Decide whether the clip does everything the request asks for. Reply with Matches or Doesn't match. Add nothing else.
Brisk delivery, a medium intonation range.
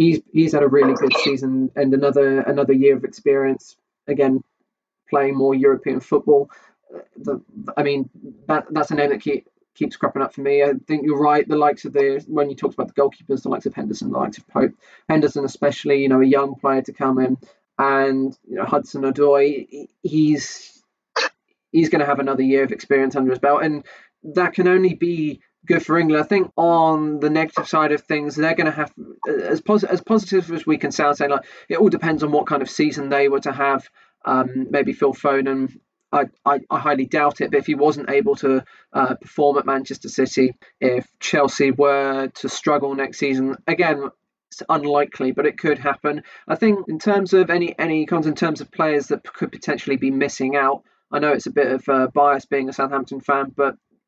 Doesn't match